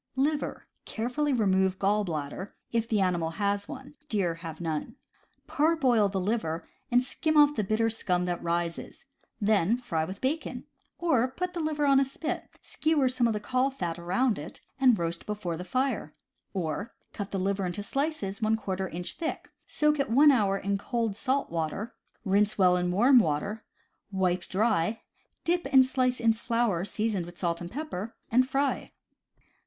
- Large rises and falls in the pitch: Yes, wide, 6.3 semitones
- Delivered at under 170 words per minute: No, average, 175 wpm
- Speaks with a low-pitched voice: No, high, 210 Hz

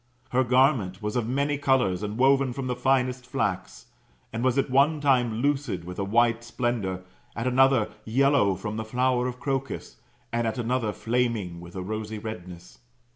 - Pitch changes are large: No, average, 3.7 semitones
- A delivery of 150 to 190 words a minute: Yes, average, 175 wpm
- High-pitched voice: No, low, 120 Hz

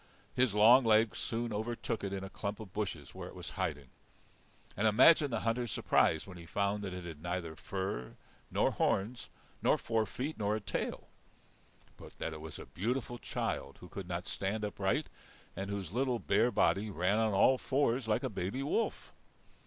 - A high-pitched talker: No, low, 105 Hz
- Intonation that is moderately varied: Yes, average, 3.8 semitones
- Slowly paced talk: No, average, 185 wpm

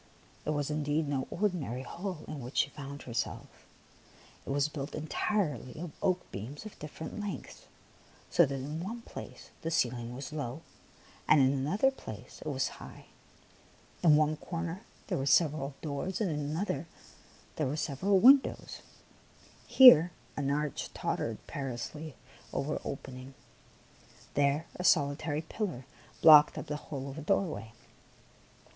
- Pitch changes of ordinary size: Yes, average, 3.6 semitones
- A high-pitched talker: No, medium, 150 Hz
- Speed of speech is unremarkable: Yes, average, 150 wpm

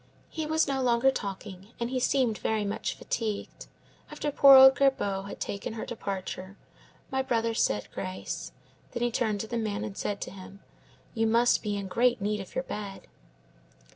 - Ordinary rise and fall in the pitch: Yes, average, 3.9 semitones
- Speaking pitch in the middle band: No, high, 220 Hz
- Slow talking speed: No, average, 180 wpm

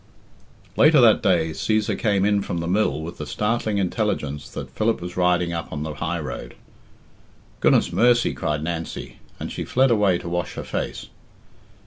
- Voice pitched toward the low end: Yes, very low, 90 Hz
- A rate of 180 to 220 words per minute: No, average, 170 wpm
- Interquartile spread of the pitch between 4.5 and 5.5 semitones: Yes, average, 4.9 semitones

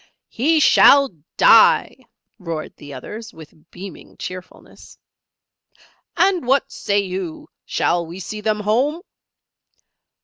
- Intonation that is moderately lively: No, wide, 7.3 semitones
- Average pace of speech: No, slow, 105 wpm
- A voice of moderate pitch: No, high, 205 Hz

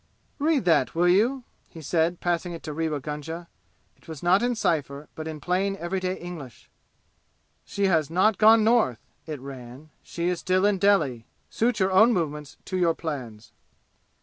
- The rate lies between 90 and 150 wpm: No, average, 170 wpm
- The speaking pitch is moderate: Yes, medium, 170 Hz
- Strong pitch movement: No, average, 4.3 semitones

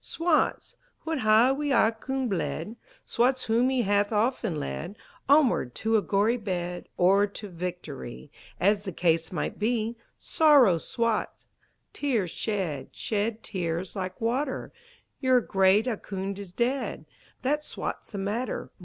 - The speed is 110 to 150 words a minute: Yes, slow, 135 wpm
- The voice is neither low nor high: No, high, 215 Hz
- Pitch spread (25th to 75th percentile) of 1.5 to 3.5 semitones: No, average, 4.7 semitones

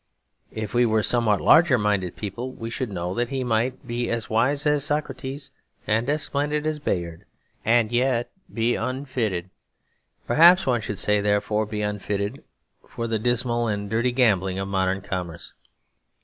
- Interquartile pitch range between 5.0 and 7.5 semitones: No, average, 4.1 semitones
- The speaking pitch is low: Yes, low, 115 Hz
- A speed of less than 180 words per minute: Yes, average, 160 wpm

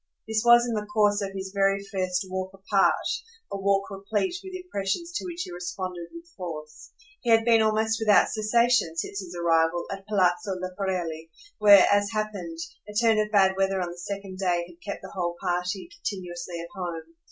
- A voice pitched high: Yes, high, 195 Hz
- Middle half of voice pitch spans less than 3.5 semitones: Yes, average, 3.0 semitones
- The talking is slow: No, average, 185 wpm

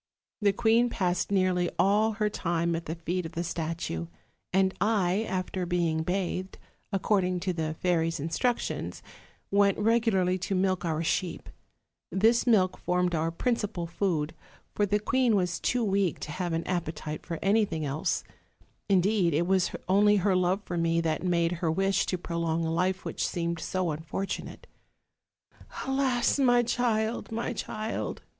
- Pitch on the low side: No, medium, 185 Hz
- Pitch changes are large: No, average, 3.6 semitones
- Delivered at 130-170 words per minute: Yes, average, 155 wpm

